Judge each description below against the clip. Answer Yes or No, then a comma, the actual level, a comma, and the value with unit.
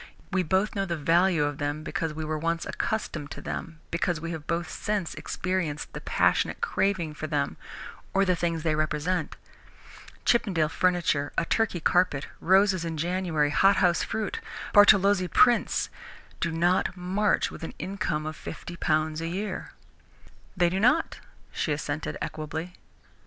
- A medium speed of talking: Yes, average, 150 wpm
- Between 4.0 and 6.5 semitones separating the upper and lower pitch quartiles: No, average, 3.3 semitones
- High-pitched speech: No, medium, 170 Hz